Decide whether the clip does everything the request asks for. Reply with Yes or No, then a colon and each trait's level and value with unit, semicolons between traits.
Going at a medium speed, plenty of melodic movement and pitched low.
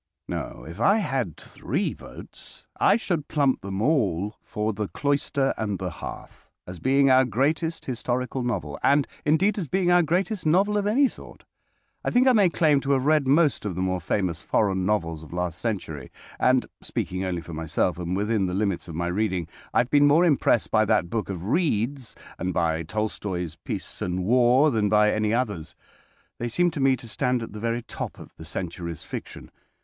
Yes: average, 195 wpm; wide, 7.6 semitones; low, 110 Hz